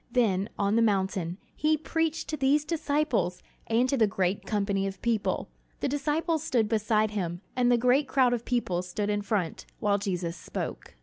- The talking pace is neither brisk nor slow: Yes, average, 180 wpm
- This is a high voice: Yes, high, 220 Hz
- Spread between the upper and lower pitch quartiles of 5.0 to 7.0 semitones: Yes, wide, 5.4 semitones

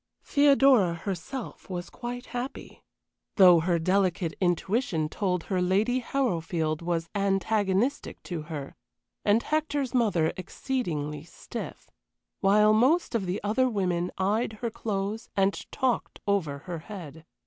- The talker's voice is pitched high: Yes, high, 195 Hz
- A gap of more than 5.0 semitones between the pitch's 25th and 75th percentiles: Yes, wide, 5.4 semitones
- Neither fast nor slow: No, slow, 125 wpm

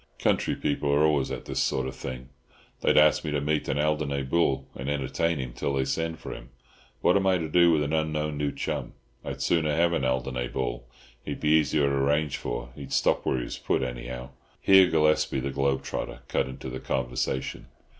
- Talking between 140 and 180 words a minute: No, fast, 205 wpm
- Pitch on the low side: Yes, very low, 70 Hz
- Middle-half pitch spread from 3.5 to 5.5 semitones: No, average, 2.8 semitones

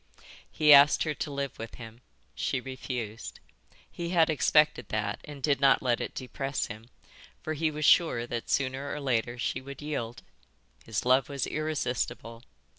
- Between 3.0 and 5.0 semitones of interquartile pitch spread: Yes, average, 3.8 semitones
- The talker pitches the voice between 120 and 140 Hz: Yes, low, 135 Hz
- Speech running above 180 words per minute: No, average, 165 wpm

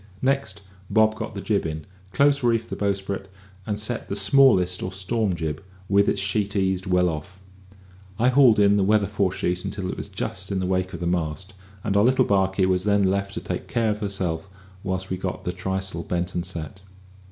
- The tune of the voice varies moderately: No, narrow, 2.2 semitones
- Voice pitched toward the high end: No, very low, 95 Hz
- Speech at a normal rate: No, fast, 210 wpm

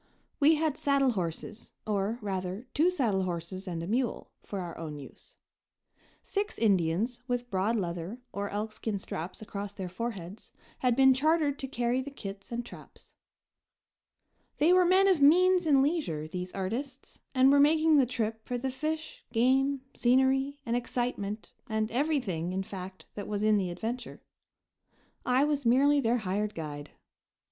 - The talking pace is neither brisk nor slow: Yes, average, 155 wpm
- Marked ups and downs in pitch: Yes, wide, 6.1 semitones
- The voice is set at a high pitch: Yes, high, 235 Hz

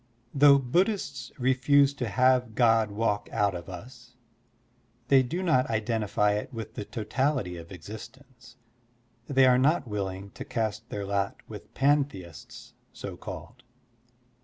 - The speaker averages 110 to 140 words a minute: Yes, slow, 135 wpm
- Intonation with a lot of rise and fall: No, average, 4.6 semitones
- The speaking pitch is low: Yes, low, 120 Hz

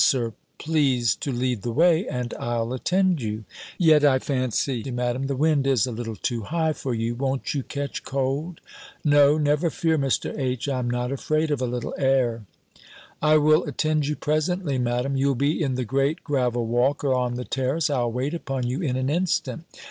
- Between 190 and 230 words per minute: Yes, average, 195 wpm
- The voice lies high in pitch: No, low, 135 Hz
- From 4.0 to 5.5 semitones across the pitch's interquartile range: No, average, 3.5 semitones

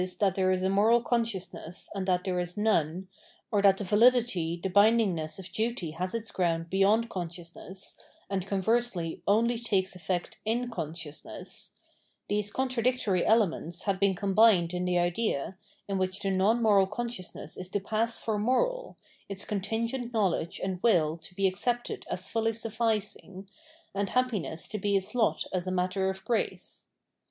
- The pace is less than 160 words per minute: No, average, 165 wpm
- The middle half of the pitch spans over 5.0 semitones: No, average, 3.7 semitones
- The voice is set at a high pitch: Yes, high, 195 Hz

